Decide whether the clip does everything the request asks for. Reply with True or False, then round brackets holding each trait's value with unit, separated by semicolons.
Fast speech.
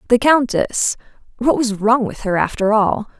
False (150 wpm)